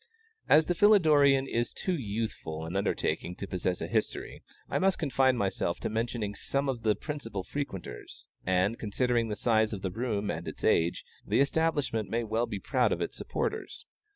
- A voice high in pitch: No, low, 115 Hz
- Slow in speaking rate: No, average, 180 wpm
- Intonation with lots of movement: Yes, wide, 5.7 semitones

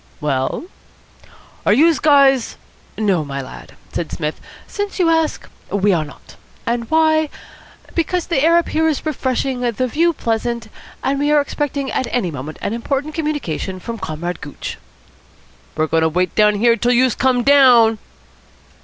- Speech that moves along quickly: No, average, 160 wpm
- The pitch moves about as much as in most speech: No, wide, 7.7 semitones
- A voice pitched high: Yes, high, 245 Hz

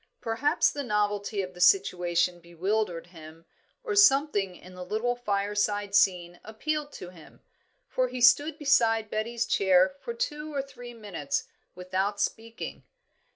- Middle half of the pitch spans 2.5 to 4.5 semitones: No, wide, 5.5 semitones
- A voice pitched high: Yes, high, 210 Hz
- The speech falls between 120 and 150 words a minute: Yes, average, 140 wpm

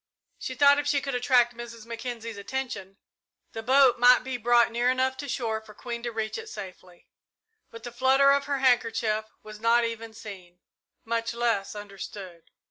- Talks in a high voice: Yes, high, 235 Hz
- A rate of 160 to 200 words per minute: Yes, average, 175 wpm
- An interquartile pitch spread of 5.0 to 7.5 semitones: No, average, 2.9 semitones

